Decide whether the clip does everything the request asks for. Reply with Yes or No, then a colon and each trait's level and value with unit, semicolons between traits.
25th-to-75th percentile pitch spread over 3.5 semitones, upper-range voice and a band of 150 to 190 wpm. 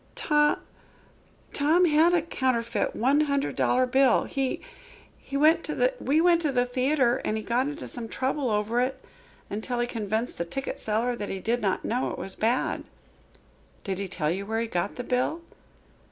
Yes: average, 4.6 semitones; very high, 250 Hz; average, 170 wpm